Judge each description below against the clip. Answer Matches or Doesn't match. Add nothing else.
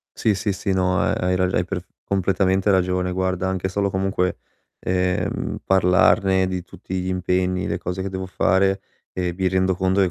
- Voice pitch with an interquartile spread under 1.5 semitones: Matches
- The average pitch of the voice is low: Matches